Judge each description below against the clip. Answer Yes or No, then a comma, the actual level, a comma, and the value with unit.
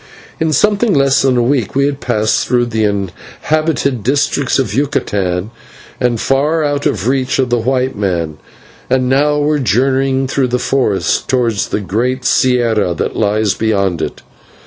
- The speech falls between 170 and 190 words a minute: No, average, 160 wpm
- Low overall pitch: Yes, low, 125 Hz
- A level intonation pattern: No, average, 4.2 semitones